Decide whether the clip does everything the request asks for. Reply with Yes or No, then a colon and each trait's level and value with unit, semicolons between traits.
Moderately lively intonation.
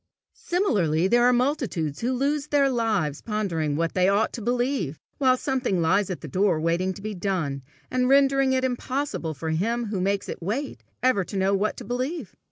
No: wide, 6.2 semitones